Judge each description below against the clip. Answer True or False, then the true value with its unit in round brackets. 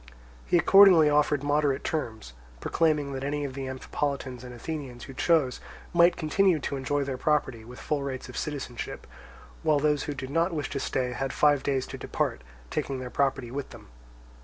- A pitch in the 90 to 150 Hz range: True (140 Hz)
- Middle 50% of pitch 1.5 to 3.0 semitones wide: True (2.5 semitones)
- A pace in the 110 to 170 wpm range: False (185 wpm)